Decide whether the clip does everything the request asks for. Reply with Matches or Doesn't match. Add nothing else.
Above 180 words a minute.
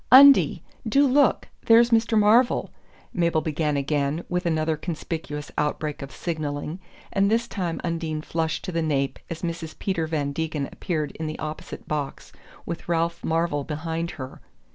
Doesn't match